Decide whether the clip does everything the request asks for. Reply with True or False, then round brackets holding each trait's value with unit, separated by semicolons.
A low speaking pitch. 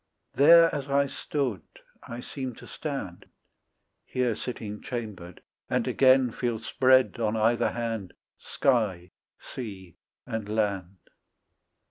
True (115 Hz)